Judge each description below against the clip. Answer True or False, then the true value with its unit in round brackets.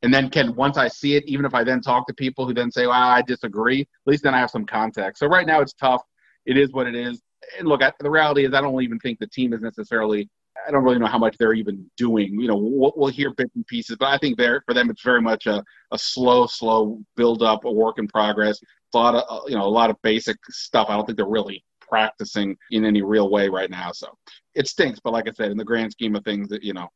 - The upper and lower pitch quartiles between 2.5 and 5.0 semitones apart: True (3.7 semitones)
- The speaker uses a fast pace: True (275 wpm)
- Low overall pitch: True (120 Hz)